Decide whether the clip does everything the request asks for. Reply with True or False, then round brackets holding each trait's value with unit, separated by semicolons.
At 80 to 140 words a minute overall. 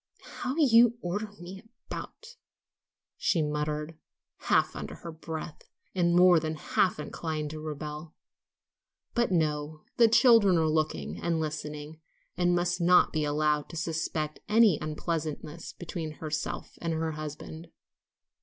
True (135 wpm)